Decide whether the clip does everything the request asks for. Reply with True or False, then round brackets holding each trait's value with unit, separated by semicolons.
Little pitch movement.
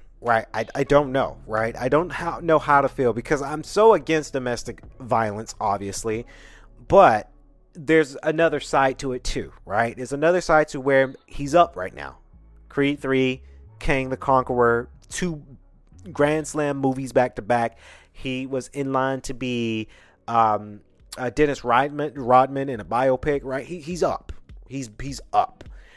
False (4.0 semitones)